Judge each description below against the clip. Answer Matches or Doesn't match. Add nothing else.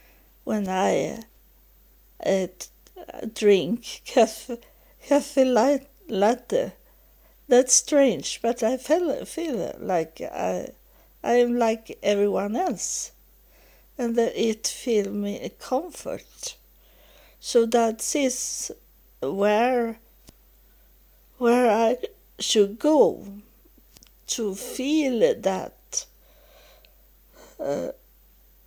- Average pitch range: Matches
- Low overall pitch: Doesn't match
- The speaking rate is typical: Doesn't match